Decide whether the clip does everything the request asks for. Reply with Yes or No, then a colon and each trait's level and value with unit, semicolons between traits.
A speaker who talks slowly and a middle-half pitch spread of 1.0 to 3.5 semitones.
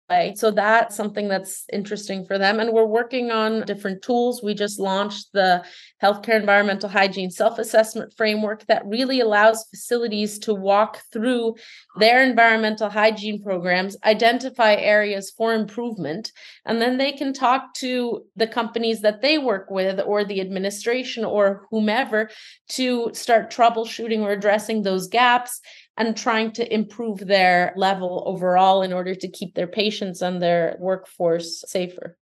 No: average, 145 wpm; average, 2.8 semitones